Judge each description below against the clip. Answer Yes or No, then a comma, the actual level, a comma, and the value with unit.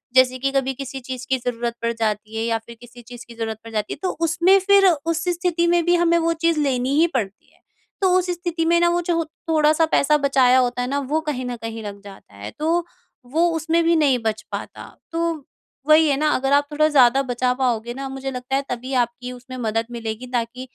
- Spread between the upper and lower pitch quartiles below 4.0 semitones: No, average, 5.3 semitones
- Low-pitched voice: No, very high, 265 Hz